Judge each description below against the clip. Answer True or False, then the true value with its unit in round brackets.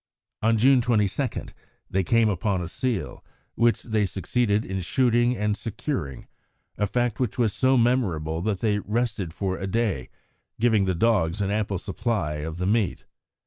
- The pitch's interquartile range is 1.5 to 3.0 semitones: False (4.1 semitones)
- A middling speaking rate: True (160 wpm)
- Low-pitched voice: True (105 Hz)